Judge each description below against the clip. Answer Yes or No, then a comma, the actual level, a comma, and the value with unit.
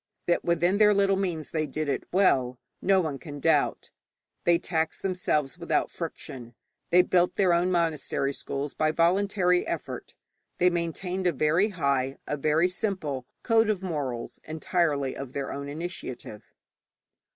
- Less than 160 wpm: Yes, average, 150 wpm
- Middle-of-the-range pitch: Yes, medium, 165 Hz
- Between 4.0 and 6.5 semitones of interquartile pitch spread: Yes, average, 4.3 semitones